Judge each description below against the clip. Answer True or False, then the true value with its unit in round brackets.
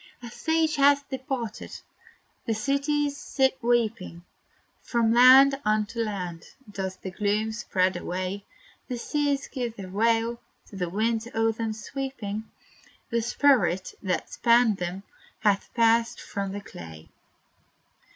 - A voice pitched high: True (225 Hz)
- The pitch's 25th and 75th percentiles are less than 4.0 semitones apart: False (4.3 semitones)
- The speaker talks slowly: True (125 wpm)